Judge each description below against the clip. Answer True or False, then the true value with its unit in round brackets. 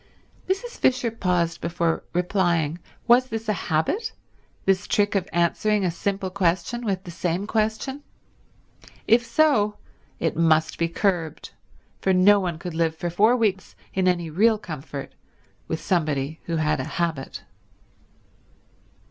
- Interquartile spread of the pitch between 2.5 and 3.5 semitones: False (4.3 semitones)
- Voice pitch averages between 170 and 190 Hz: True (185 Hz)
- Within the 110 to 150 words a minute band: True (140 wpm)